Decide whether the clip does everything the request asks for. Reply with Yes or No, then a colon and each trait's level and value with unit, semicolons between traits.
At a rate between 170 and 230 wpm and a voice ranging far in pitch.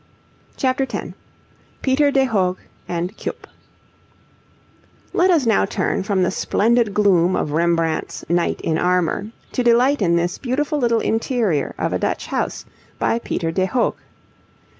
No: average, 140 wpm; wide, 6.4 semitones